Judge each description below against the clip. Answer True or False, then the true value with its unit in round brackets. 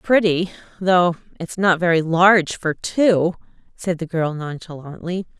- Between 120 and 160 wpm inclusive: True (135 wpm)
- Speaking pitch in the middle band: True (175 Hz)